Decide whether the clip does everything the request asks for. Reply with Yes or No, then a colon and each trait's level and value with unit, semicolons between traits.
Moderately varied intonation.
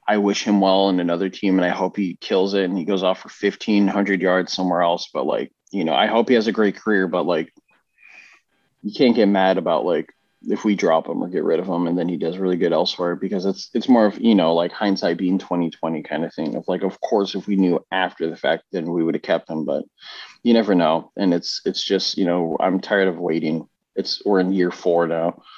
No: narrow, 2.3 semitones